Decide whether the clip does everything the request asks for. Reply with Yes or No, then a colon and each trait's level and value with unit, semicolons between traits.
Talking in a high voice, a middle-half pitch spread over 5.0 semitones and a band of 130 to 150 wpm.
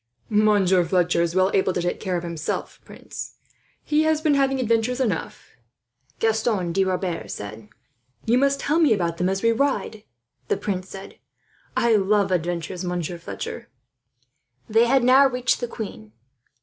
No: high, 200 Hz; wide, 5.4 semitones; average, 160 wpm